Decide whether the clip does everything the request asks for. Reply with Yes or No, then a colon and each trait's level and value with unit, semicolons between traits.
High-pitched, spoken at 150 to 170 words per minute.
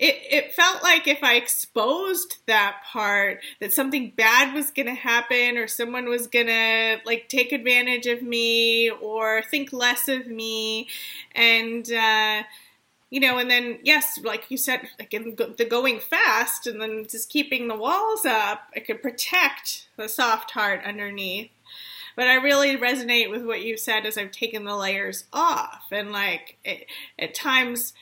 Yes: high, 235 Hz; average, 165 wpm